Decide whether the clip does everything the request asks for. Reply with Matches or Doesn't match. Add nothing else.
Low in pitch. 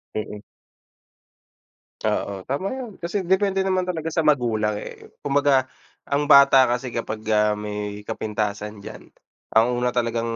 Matches